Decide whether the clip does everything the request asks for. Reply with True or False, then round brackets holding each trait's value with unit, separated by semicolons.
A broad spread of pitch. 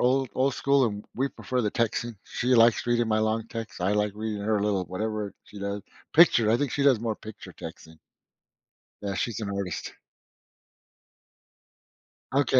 False (2.9 semitones)